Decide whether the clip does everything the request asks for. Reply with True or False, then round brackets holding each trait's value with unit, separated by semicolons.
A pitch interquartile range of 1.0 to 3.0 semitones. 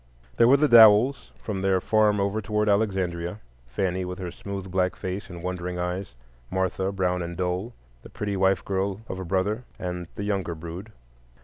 True (2.4 semitones)